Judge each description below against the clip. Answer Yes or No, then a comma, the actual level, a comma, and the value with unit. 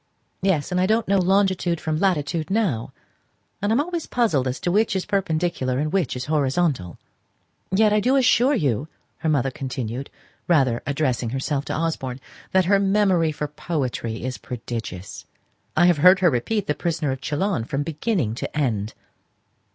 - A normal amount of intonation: No, wide, 6.5 semitones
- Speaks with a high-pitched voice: No, medium, 155 Hz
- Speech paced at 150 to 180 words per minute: Yes, average, 165 wpm